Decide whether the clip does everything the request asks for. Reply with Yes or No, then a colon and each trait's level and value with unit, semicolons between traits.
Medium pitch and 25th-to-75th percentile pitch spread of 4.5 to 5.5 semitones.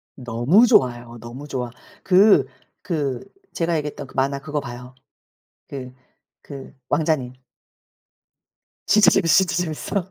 Yes: medium, 145 Hz; average, 5.2 semitones